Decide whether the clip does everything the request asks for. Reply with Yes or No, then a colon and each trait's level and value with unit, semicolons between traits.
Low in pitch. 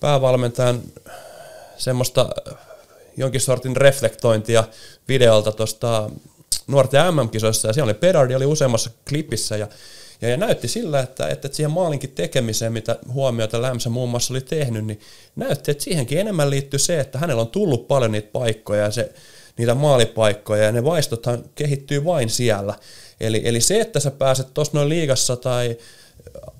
Yes: low, 125 Hz